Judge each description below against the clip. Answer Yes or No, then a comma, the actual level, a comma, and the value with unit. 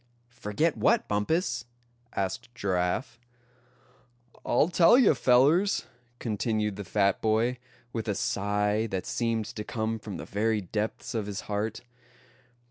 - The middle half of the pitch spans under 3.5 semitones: Yes, average, 2.9 semitones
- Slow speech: Yes, slow, 125 wpm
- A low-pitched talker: Yes, low, 110 Hz